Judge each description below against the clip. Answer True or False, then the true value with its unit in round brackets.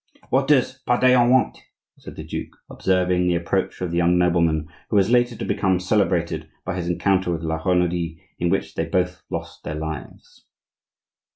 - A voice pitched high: False (90 Hz)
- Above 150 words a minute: True (175 wpm)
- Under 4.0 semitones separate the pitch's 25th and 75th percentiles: True (2.5 semitones)